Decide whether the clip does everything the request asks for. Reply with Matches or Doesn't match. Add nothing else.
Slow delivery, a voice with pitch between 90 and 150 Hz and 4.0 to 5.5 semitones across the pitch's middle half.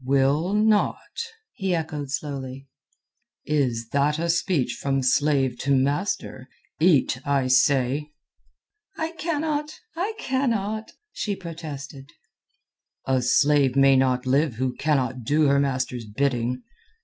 Matches